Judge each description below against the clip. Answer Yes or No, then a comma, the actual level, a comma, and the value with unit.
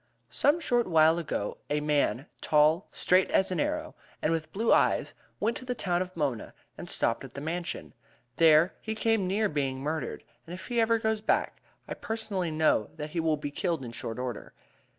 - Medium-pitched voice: Yes, medium, 165 Hz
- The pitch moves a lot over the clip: Yes, wide, 5.7 semitones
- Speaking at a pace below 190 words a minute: No, average, 195 wpm